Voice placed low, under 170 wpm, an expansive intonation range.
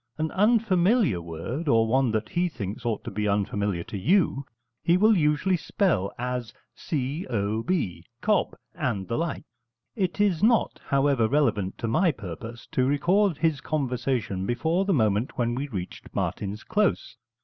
Yes: low, 130 Hz; average, 160 wpm; wide, 8.2 semitones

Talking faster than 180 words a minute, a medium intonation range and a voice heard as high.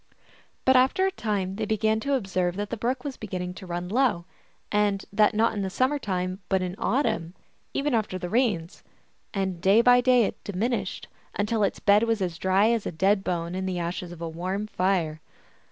Yes: average, 200 wpm; average, 3.9 semitones; high, 200 Hz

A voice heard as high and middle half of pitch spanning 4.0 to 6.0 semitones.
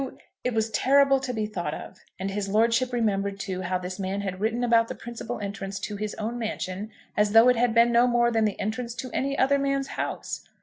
No: high, 225 Hz; average, 3.4 semitones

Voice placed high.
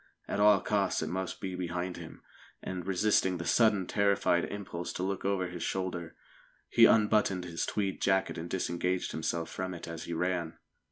No: very low, 95 Hz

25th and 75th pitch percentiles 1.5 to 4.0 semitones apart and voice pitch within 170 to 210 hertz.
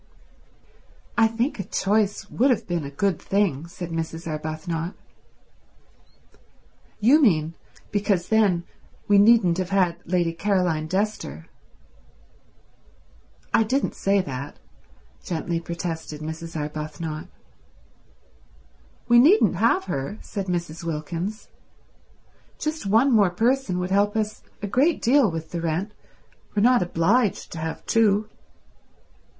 No: average, 4.7 semitones; medium, 185 Hz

